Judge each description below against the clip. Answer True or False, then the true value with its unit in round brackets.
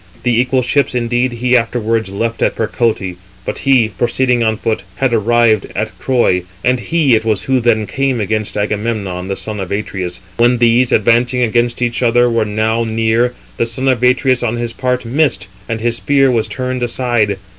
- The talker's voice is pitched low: True (115 Hz)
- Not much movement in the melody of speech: True (2.2 semitones)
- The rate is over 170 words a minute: True (185 wpm)